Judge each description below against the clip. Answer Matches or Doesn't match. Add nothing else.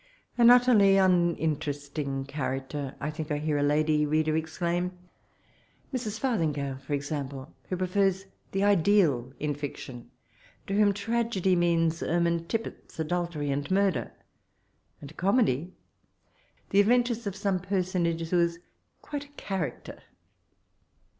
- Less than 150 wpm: Matches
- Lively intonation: Doesn't match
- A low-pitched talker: Doesn't match